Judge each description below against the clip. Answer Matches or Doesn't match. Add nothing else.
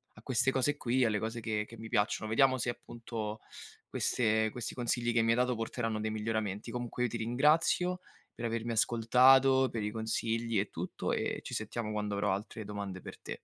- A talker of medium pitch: Doesn't match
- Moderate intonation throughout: Doesn't match